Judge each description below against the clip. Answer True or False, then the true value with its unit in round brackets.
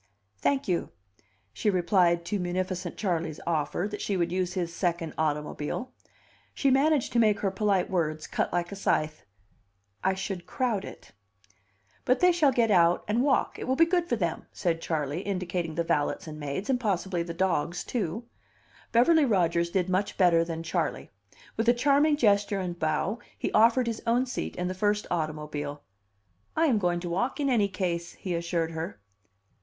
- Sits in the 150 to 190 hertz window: True (185 Hz)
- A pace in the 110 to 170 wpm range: False (180 wpm)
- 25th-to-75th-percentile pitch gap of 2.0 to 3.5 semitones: False (5.0 semitones)